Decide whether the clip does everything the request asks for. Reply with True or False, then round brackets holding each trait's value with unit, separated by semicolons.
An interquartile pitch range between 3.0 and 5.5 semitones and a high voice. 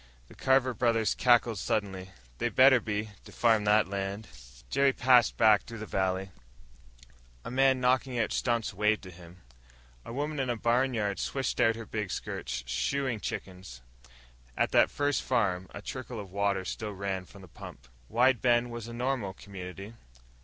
False (4.2 semitones; 110 Hz)